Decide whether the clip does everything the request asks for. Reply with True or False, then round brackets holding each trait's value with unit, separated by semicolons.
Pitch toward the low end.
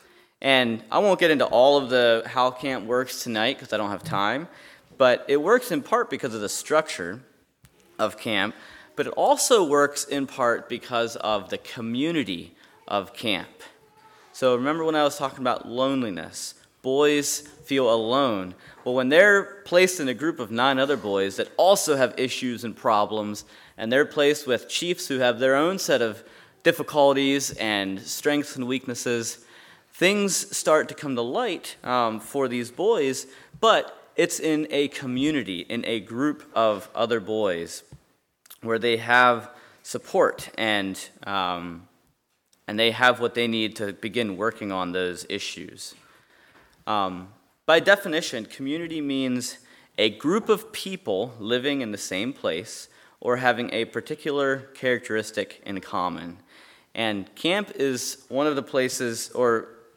True (125 Hz)